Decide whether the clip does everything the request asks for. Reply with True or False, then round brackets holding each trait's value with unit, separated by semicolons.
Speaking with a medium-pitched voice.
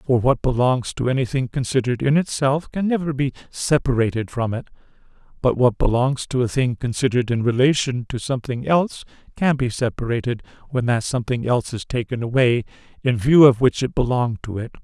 False (125 Hz)